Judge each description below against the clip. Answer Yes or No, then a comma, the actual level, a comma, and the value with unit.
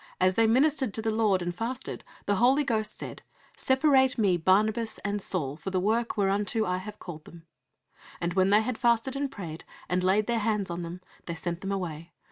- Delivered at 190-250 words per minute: Yes, fast, 205 wpm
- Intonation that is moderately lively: Yes, average, 4.0 semitones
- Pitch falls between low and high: No, high, 205 Hz